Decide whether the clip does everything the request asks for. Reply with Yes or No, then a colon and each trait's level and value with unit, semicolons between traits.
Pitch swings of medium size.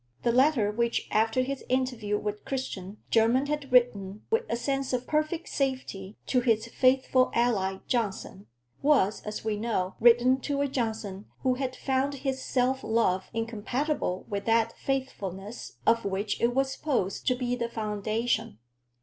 Yes: average, 3.8 semitones